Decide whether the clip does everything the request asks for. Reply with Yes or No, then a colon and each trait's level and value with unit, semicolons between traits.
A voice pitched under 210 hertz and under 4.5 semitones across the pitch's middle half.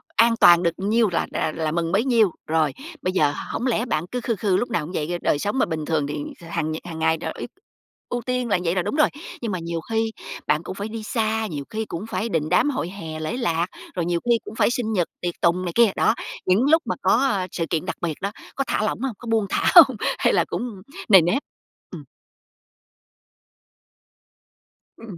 No: high, 190 Hz; average, 5.3 semitones